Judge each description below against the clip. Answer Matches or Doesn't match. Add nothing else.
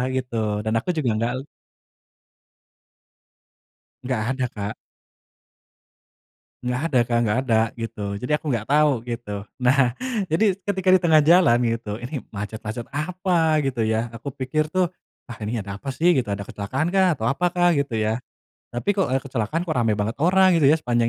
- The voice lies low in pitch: Matches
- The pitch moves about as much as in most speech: Doesn't match